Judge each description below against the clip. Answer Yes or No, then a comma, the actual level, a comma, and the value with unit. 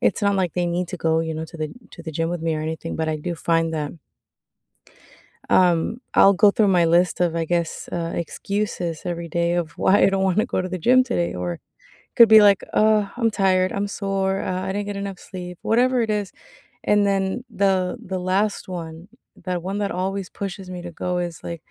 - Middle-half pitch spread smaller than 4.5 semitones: Yes, average, 2.9 semitones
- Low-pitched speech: No, medium, 185 Hz